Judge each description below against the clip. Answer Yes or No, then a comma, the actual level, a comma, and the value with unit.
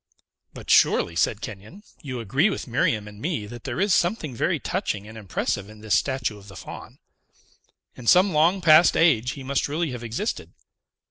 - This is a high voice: No, low, 125 Hz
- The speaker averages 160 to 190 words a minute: Yes, average, 185 wpm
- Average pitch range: No, wide, 7.2 semitones